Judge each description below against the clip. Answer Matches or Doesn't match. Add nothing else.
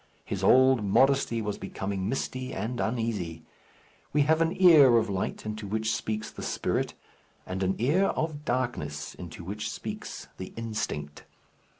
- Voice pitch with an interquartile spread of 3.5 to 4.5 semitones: Doesn't match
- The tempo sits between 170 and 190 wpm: Doesn't match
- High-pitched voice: Doesn't match